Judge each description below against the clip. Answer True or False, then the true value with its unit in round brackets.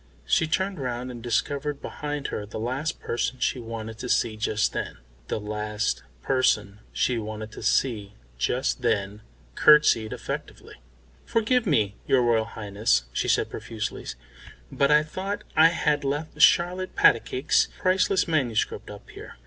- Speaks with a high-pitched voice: False (125 Hz)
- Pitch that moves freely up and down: True (5.7 semitones)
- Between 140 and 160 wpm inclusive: True (145 wpm)